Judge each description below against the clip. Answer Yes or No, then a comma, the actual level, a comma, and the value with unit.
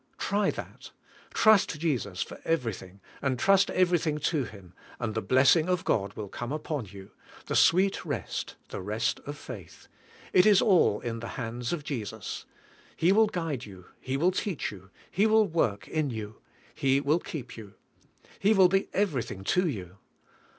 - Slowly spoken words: No, average, 175 wpm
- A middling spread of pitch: No, wide, 8.7 semitones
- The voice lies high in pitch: No, medium, 140 Hz